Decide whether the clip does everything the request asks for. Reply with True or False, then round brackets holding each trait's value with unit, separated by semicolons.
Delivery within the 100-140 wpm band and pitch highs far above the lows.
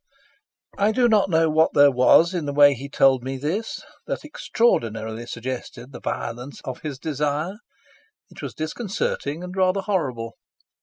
False (155 wpm; 6.0 semitones)